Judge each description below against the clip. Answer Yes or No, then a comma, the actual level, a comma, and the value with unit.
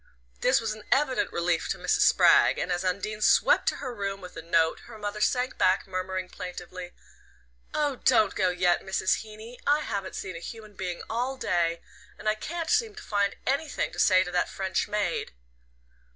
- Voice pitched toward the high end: Yes, high, 200 Hz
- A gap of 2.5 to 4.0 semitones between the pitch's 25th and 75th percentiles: No, average, 4.6 semitones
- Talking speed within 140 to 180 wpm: No, average, 190 wpm